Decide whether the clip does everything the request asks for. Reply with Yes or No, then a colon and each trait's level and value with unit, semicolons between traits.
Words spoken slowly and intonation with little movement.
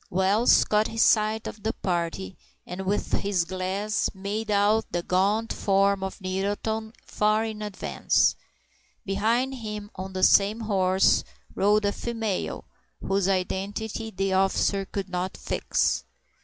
Yes: slow, 130 wpm; narrow, 2.2 semitones